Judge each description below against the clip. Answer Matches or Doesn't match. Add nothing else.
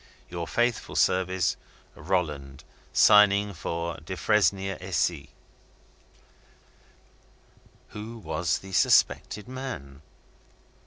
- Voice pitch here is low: Matches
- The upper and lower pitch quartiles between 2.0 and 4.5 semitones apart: Matches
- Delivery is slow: Matches